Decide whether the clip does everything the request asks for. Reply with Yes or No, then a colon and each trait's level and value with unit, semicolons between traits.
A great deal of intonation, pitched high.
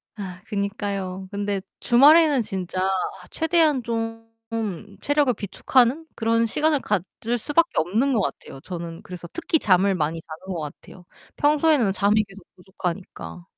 Yes: wide, 6.2 semitones; high, 205 Hz